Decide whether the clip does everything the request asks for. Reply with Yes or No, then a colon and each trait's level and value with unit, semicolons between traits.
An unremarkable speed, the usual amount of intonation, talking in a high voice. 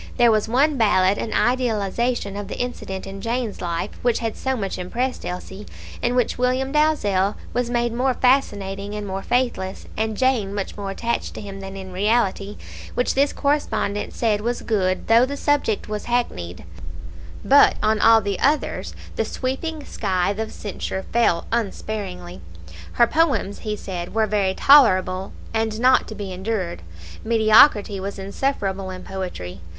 Yes: average, 160 wpm; average, 4.0 semitones; high, 215 Hz